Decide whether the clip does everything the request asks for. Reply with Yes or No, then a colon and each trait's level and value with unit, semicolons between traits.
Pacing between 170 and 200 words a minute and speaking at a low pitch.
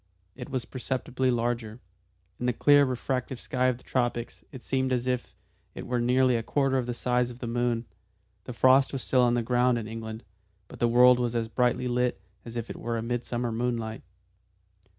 Yes: average, 190 wpm; low, 125 Hz